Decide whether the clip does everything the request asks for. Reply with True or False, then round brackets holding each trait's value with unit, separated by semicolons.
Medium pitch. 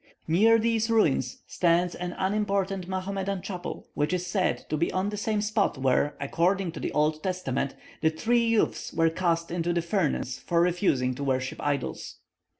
True (180 Hz)